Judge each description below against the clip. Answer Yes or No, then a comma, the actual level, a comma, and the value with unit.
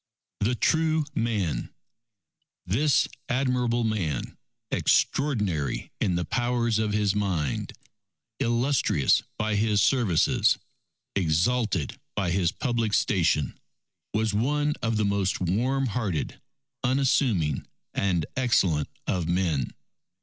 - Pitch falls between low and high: No, low, 105 Hz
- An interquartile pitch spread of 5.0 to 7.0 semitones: Yes, wide, 5.6 semitones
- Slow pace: Yes, slow, 100 wpm